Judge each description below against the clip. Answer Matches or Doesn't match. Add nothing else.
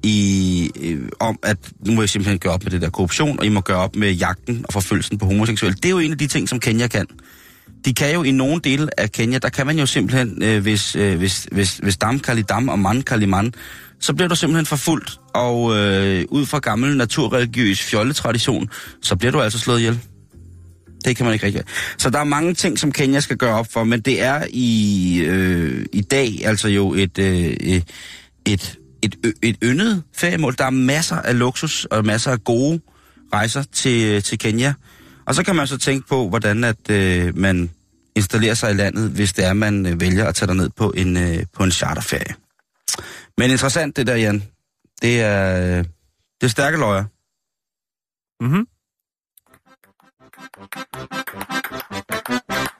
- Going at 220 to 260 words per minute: Doesn't match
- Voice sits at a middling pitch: Doesn't match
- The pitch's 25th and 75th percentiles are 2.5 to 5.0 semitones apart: Doesn't match